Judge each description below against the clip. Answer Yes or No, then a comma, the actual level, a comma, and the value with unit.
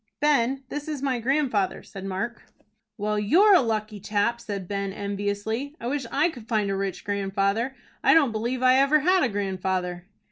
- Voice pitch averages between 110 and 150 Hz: No, high, 220 Hz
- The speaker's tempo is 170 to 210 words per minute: Yes, average, 180 wpm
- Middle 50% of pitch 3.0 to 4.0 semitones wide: No, average, 5.2 semitones